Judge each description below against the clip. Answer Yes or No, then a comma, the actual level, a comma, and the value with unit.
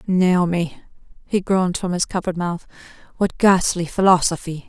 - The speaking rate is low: Yes, slow, 130 wpm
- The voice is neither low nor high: Yes, medium, 180 Hz